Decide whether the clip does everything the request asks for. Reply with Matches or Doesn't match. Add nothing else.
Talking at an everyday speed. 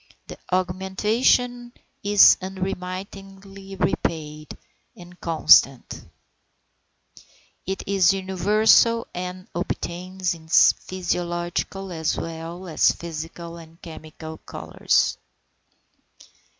Doesn't match